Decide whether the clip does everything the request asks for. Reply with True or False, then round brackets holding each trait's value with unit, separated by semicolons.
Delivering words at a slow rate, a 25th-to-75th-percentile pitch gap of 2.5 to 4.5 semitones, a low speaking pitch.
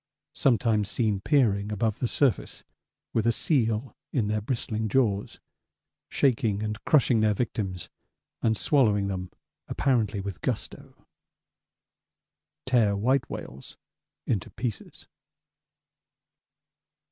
True (100 wpm; 3.3 semitones; 110 Hz)